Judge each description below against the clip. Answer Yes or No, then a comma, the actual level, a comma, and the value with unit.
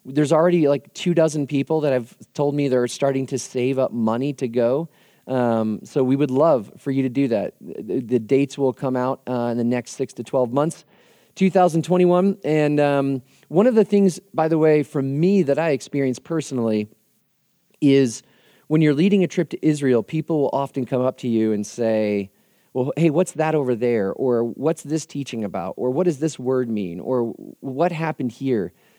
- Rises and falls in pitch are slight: No, average, 4.2 semitones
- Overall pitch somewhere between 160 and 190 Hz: No, medium, 140 Hz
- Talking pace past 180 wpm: Yes, average, 200 wpm